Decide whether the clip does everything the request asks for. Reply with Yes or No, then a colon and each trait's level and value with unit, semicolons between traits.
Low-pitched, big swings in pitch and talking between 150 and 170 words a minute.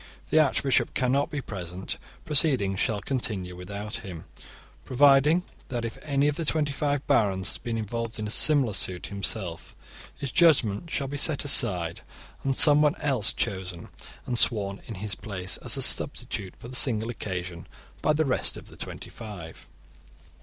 Yes: low, 115 Hz; wide, 6.4 semitones; average, 165 wpm